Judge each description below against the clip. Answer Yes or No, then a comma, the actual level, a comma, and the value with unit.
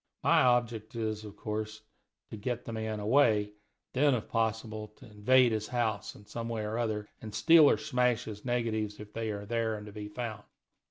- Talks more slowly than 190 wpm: No, fast, 205 wpm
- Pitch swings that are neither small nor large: No, narrow, 1.9 semitones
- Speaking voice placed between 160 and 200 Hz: No, low, 110 Hz